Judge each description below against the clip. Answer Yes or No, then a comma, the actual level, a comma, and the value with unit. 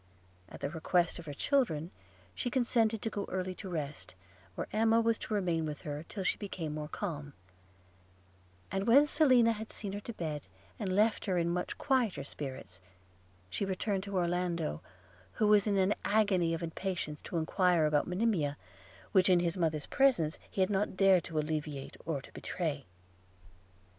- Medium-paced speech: Yes, average, 175 wpm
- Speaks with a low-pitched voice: No, medium, 180 Hz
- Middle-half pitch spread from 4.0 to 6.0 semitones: Yes, average, 4.9 semitones